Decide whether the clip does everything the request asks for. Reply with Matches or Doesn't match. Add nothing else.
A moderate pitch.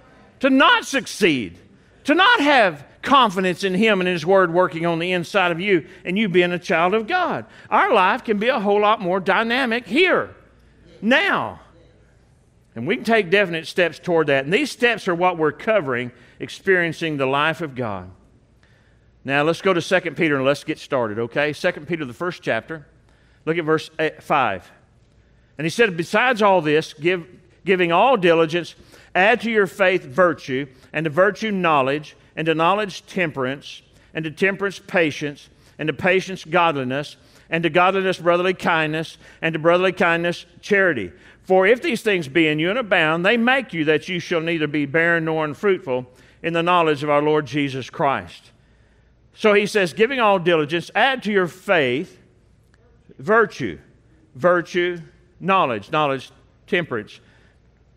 Matches